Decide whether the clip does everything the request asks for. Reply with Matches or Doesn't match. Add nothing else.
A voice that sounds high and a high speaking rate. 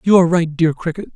Doesn't match